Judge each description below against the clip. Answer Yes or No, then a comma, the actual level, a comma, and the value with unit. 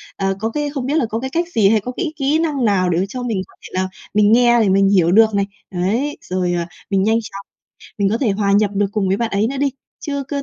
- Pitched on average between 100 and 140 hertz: No, high, 215 Hz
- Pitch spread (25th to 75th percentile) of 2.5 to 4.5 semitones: No, average, 5.0 semitones